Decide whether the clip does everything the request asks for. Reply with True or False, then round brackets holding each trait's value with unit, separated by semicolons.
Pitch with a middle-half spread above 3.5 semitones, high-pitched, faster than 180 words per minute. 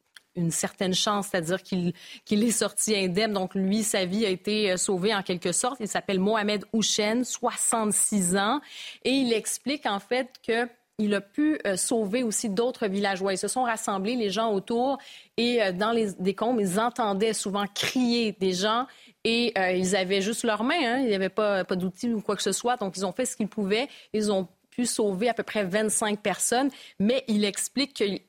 False (3.2 semitones; 215 Hz; 200 wpm)